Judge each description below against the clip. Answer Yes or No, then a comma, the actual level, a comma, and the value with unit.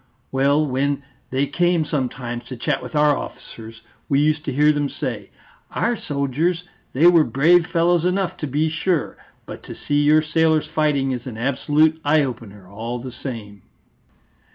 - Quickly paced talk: No, average, 165 wpm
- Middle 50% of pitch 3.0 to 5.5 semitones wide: Yes, average, 3.6 semitones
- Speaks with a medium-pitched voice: Yes, medium, 145 Hz